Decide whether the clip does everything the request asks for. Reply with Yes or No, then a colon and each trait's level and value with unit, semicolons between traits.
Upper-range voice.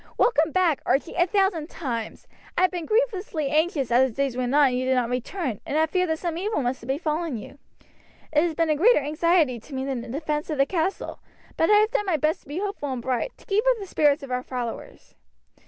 Yes: very high, 305 Hz